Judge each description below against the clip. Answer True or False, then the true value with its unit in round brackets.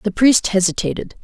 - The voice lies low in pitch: False (205 Hz)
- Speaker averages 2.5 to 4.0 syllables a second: False (5.5 syllables/s)